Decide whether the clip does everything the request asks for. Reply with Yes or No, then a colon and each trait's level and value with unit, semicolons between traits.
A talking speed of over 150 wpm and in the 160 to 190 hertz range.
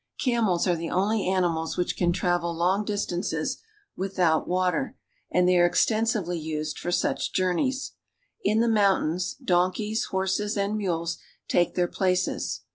No: average, 145 wpm; medium, 185 Hz